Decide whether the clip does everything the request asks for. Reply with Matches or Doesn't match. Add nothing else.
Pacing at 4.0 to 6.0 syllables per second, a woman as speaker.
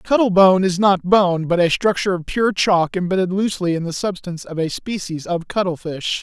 Doesn't match